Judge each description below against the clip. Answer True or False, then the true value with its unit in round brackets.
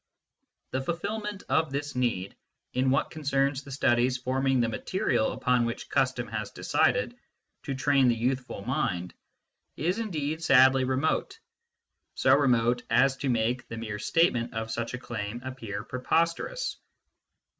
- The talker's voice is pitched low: True (130 Hz)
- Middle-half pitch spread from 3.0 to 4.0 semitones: True (3.4 semitones)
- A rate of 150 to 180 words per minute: False (140 wpm)